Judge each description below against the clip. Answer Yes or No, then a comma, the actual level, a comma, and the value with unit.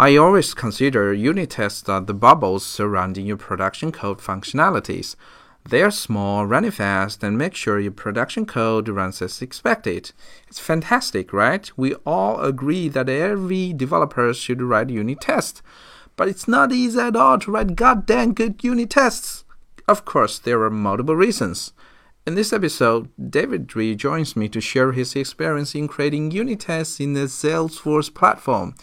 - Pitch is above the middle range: No, low, 135 Hz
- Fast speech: No, average, 160 wpm